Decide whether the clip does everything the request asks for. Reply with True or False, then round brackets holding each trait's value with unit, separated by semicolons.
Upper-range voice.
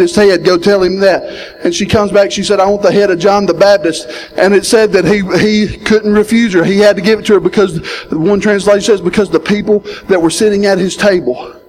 True (200 Hz)